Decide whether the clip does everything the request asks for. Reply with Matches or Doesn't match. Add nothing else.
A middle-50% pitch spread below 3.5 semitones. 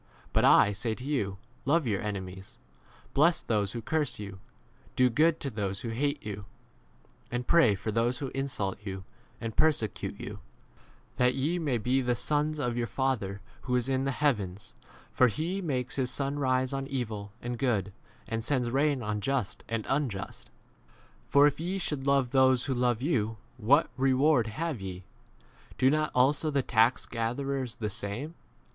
Doesn't match